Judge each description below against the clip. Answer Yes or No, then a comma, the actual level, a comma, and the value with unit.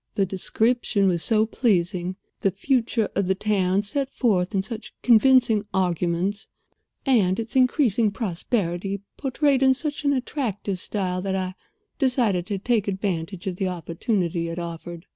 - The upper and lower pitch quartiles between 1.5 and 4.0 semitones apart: No, average, 4.7 semitones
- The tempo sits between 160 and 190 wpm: No, average, 145 wpm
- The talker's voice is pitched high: Yes, high, 200 Hz